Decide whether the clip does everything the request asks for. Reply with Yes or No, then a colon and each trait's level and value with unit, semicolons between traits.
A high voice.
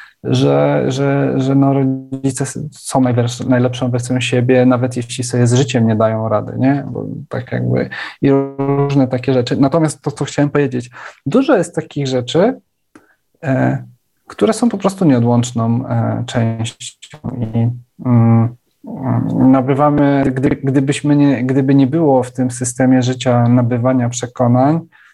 No: low, 130 Hz